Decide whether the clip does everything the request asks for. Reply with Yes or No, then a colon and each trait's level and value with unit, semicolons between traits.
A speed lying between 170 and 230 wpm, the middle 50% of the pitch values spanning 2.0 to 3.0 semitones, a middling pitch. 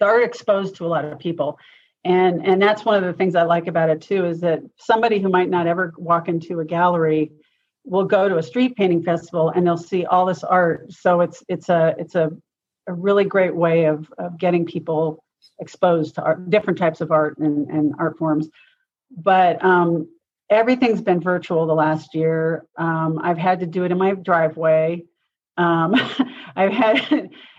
Yes: average, 190 wpm; average, 2.7 semitones; medium, 175 Hz